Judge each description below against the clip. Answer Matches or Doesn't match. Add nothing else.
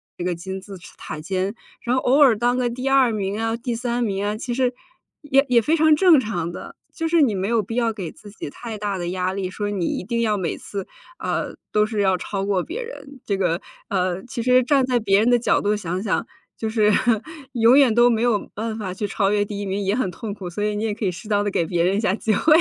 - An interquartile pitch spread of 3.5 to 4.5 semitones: Matches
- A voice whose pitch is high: Matches